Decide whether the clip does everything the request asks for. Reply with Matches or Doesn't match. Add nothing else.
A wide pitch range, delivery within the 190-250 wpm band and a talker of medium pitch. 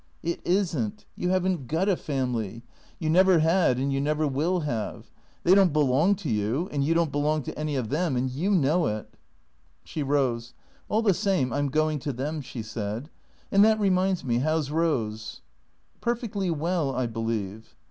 Matches